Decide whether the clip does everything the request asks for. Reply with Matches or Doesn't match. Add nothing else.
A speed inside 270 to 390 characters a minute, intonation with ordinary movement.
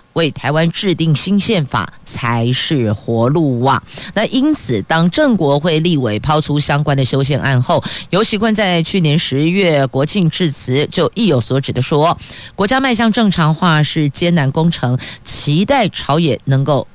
Doesn't match